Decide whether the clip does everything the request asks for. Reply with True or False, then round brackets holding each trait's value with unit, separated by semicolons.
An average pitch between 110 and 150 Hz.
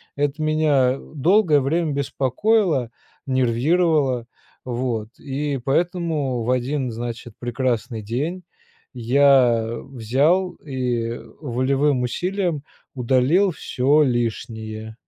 True (135 Hz)